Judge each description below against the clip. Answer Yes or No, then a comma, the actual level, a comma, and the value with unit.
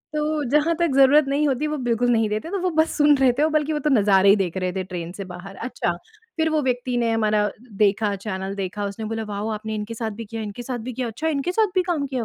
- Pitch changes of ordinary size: No, wide, 6.4 semitones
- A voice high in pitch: Yes, high, 235 Hz